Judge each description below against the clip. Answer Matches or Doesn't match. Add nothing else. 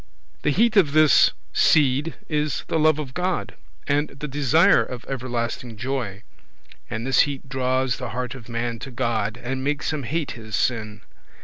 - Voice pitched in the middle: Doesn't match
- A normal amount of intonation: Matches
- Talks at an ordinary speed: Matches